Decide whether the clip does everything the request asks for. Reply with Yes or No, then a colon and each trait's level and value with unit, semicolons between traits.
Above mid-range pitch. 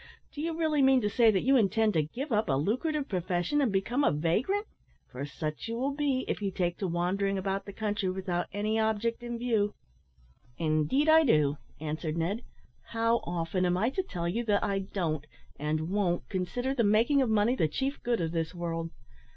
Yes: high, 205 Hz